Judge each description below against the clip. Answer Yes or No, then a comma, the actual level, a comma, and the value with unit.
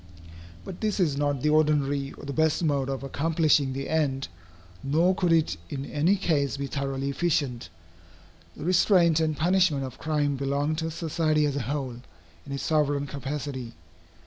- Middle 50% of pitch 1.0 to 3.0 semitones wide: Yes, narrow, 2.6 semitones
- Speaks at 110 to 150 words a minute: No, average, 165 wpm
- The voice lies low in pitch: No, medium, 145 Hz